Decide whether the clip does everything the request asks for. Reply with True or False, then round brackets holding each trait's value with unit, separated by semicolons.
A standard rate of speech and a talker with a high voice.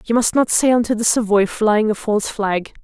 False (235 wpm; 220 Hz)